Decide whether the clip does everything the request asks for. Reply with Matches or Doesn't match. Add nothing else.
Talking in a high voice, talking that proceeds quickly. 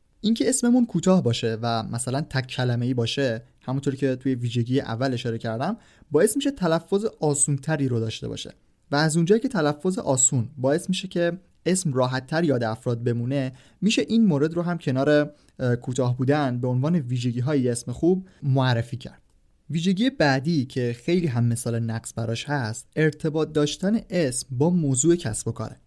Doesn't match